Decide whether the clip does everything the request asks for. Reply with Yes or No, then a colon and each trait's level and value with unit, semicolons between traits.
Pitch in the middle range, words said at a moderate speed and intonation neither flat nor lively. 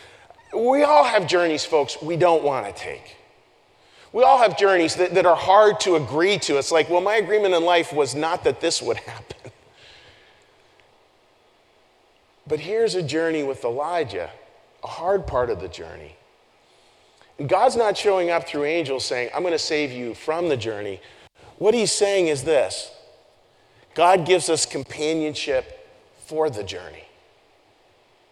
Yes: medium, 165 Hz; average, 155 wpm; average, 4.5 semitones